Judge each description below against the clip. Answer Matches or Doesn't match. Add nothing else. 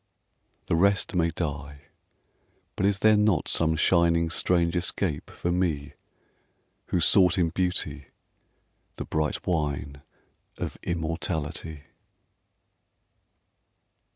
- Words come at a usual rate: Doesn't match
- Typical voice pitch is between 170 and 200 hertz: Doesn't match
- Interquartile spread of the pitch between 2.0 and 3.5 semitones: Matches